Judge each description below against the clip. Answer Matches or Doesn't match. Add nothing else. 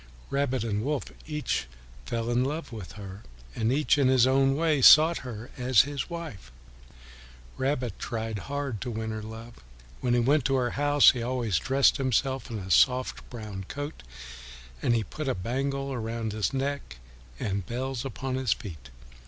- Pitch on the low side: Matches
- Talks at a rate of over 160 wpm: Matches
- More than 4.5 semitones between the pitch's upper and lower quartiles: Doesn't match